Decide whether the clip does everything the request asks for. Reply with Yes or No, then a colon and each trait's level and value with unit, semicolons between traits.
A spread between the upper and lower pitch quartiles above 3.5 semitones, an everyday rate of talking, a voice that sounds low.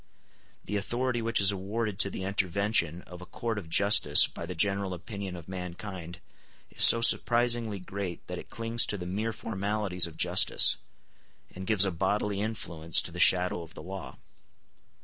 No: average, 3.1 semitones; average, 170 wpm; low, 100 Hz